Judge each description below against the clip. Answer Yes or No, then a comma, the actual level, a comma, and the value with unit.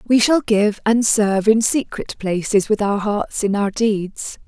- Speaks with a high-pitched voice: Yes, high, 210 Hz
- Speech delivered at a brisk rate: No, average, 190 wpm